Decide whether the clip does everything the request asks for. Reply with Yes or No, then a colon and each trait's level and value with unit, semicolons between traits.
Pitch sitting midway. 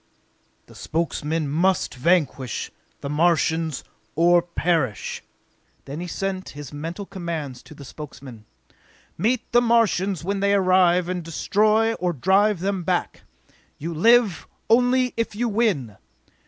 Yes: medium, 175 Hz